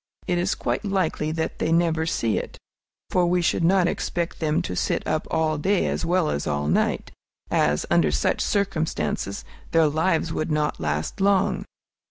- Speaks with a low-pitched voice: No, medium, 160 Hz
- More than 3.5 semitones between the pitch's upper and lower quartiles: No, average, 3.2 semitones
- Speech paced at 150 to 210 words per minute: Yes, average, 175 wpm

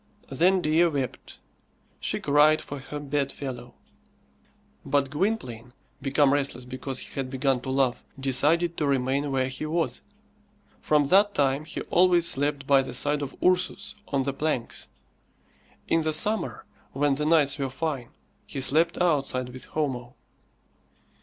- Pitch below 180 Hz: Yes, medium, 140 Hz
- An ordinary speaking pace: Yes, average, 145 wpm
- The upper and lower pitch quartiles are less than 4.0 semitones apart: Yes, average, 2.8 semitones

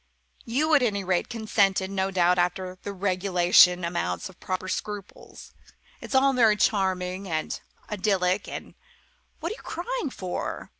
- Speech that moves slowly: No, average, 145 wpm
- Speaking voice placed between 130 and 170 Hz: No, high, 190 Hz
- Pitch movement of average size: Yes, average, 3.1 semitones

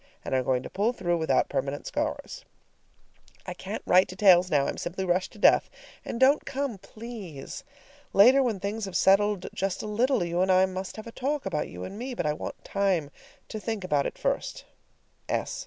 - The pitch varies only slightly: No, average, 4.3 semitones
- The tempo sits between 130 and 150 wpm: No, average, 195 wpm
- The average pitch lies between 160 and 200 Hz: Yes, high, 190 Hz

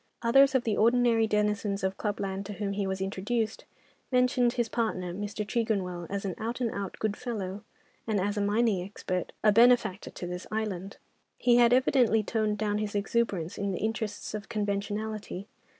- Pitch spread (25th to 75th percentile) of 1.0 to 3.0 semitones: Yes, narrow, 2.6 semitones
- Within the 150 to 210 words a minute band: Yes, average, 180 wpm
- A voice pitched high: Yes, high, 210 Hz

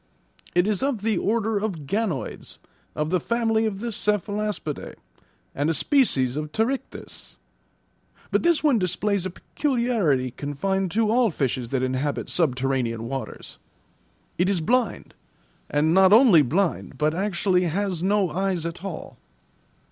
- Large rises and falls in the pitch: Yes, wide, 6.1 semitones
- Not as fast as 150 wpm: Yes, average, 140 wpm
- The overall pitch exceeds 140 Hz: Yes, high, 190 Hz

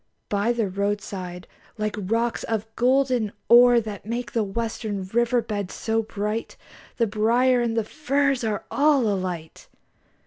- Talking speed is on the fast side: No, average, 140 wpm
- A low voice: No, high, 225 Hz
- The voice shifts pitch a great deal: No, average, 2.9 semitones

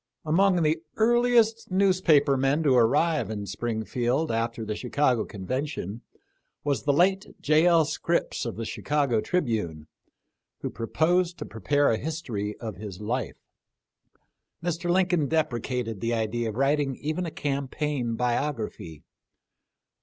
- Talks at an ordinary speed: No, slow, 130 wpm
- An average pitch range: No, wide, 6.1 semitones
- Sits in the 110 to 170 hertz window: Yes, medium, 140 Hz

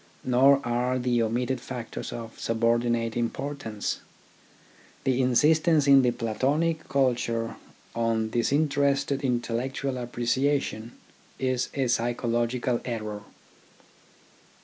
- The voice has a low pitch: Yes, low, 125 Hz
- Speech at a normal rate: No, slow, 100 wpm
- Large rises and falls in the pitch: No, average, 2.7 semitones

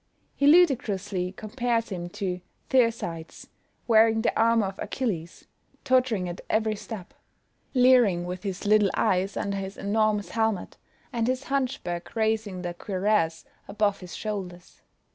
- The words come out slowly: Yes, slow, 130 wpm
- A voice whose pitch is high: Yes, high, 210 Hz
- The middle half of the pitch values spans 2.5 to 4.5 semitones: Yes, average, 3.8 semitones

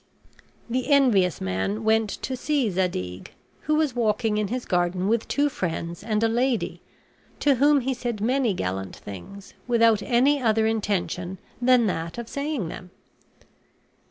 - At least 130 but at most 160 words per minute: Yes, average, 150 wpm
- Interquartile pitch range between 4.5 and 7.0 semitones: Yes, wide, 5.6 semitones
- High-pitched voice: Yes, high, 220 Hz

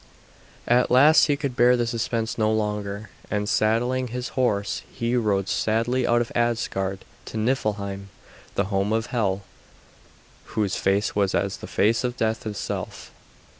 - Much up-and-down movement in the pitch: No, average, 3.1 semitones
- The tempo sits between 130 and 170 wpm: Yes, average, 150 wpm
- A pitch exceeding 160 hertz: No, low, 110 Hz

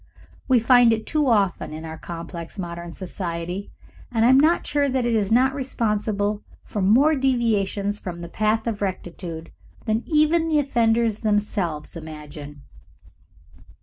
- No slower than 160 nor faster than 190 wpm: No, average, 150 wpm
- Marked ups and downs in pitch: Yes, wide, 6.0 semitones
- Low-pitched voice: No, high, 210 Hz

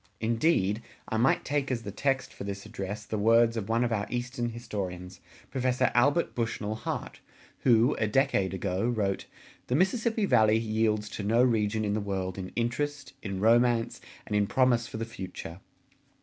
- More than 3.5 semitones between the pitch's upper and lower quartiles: No, average, 3.1 semitones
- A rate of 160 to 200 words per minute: Yes, average, 175 wpm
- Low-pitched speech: Yes, low, 115 Hz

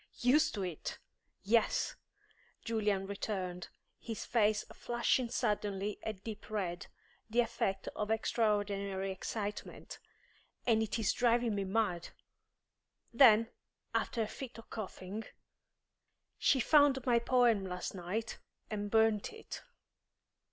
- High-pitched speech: Yes, high, 215 Hz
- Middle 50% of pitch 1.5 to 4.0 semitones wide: Yes, average, 2.8 semitones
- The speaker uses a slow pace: Yes, slow, 115 wpm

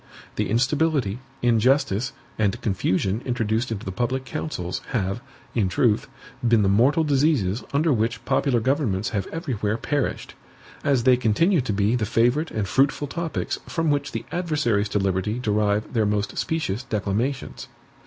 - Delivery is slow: No, average, 150 wpm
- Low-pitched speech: Yes, low, 120 Hz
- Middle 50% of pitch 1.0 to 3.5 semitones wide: No, average, 5.1 semitones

